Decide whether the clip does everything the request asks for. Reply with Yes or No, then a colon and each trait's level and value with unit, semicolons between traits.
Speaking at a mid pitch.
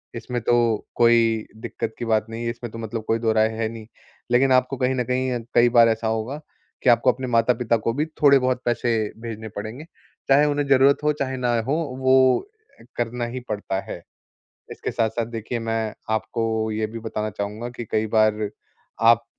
No: low, 115 Hz